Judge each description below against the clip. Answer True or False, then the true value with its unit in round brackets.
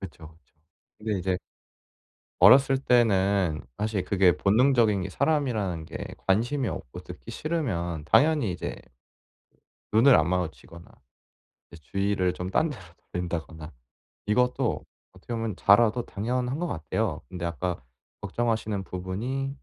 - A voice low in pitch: True (100 Hz)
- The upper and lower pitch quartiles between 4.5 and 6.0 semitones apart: True (5.5 semitones)